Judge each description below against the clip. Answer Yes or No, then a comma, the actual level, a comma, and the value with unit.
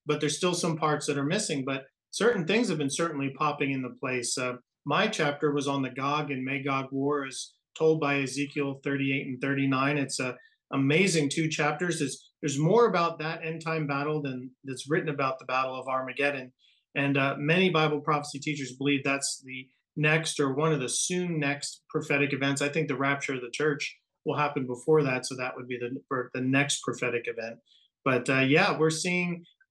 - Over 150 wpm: Yes, average, 200 wpm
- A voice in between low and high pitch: Yes, medium, 145 Hz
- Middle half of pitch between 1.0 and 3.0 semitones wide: Yes, narrow, 2.6 semitones